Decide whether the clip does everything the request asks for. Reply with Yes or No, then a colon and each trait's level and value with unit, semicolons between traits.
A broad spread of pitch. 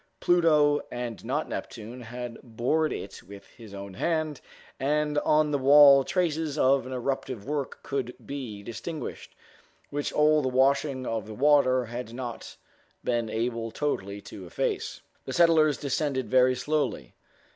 No: average, 4.0 semitones